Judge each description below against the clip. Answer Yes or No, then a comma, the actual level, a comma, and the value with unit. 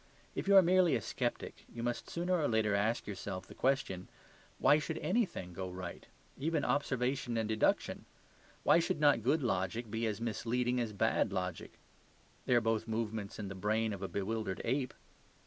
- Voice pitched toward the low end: Yes, low, 115 Hz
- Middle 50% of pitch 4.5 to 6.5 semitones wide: Yes, average, 4.9 semitones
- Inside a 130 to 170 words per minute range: No, average, 180 wpm